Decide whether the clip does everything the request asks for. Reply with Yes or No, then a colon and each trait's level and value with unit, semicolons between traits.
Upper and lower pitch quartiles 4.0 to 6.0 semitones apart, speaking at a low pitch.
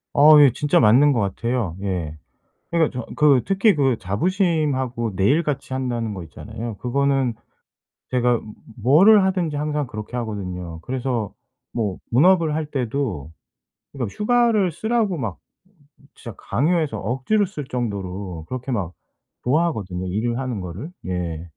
No: wide, 6.7 semitones; low, 125 Hz